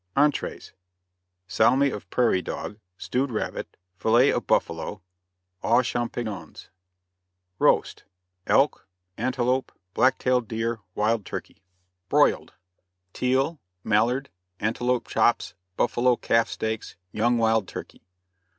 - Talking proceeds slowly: Yes, slow, 100 wpm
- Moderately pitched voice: No, low, 120 Hz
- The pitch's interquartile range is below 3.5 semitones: Yes, narrow, 2.4 semitones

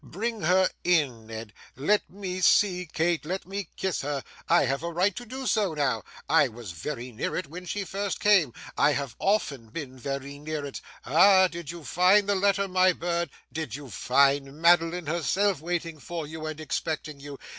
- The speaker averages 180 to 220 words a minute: Yes, average, 190 wpm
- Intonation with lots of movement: No, average, 4.9 semitones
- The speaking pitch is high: No, medium, 165 Hz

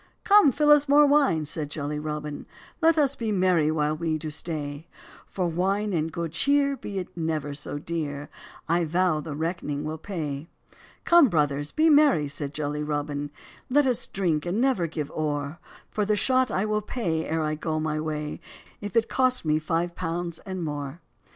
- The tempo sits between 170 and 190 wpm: Yes, average, 185 wpm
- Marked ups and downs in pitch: Yes, wide, 5.7 semitones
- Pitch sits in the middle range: Yes, medium, 165 Hz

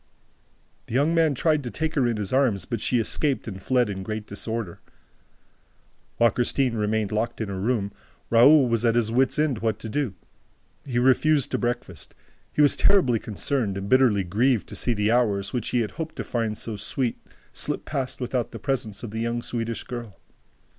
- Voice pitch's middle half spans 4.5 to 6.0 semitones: No, average, 3.5 semitones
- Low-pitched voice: Yes, low, 120 Hz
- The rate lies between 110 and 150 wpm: No, average, 195 wpm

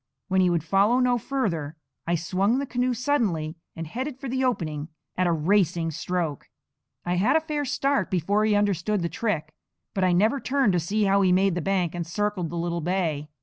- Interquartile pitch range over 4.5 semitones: Yes, wide, 5.4 semitones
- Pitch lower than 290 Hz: Yes, high, 190 Hz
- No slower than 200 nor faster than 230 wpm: Yes, fast, 205 wpm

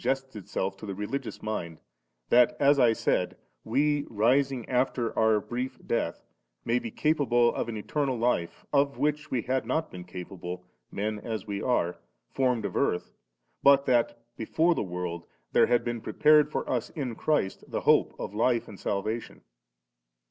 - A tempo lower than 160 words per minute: No, average, 170 wpm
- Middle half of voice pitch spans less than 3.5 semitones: No, average, 4.4 semitones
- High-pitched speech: No, low, 120 Hz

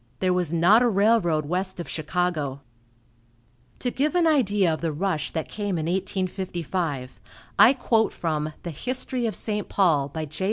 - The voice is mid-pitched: Yes, medium, 180 Hz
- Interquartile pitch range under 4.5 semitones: No, average, 4.9 semitones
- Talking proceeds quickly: No, average, 165 wpm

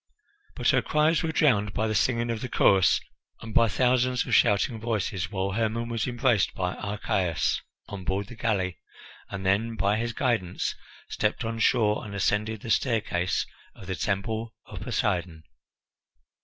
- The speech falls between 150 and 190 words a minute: Yes, average, 160 wpm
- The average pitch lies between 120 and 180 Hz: No, low, 110 Hz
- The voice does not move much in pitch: No, average, 3.1 semitones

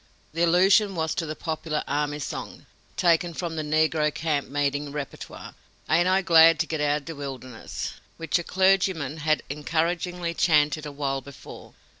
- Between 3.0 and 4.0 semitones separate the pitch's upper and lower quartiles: No, narrow, 2.5 semitones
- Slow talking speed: No, average, 160 wpm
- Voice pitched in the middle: Yes, medium, 160 Hz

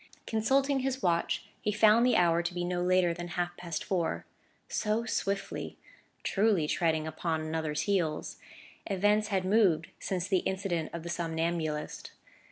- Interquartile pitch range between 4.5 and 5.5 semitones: No, average, 3.7 semitones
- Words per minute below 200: Yes, average, 155 wpm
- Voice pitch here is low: No, medium, 180 Hz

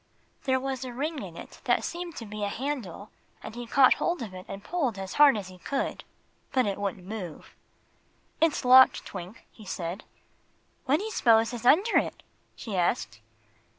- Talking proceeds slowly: No, average, 185 wpm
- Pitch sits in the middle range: No, high, 230 Hz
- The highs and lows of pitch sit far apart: Yes, wide, 5.8 semitones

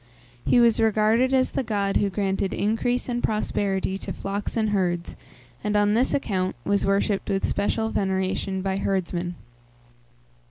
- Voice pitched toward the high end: Yes, high, 200 Hz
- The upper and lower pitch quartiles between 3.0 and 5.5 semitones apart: No, narrow, 2.5 semitones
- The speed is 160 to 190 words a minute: No, average, 150 wpm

